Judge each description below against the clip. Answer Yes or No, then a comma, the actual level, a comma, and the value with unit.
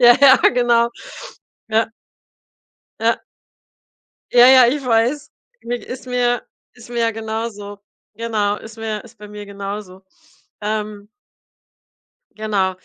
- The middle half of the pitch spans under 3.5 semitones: Yes, narrow, 2.6 semitones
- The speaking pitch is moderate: No, high, 225 Hz